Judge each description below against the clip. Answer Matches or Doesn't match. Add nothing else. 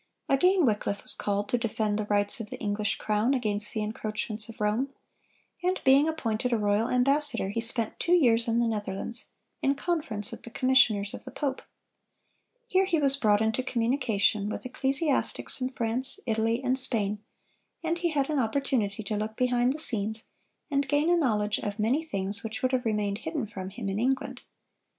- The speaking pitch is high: Matches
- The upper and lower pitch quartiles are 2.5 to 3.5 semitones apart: Doesn't match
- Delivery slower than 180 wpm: Doesn't match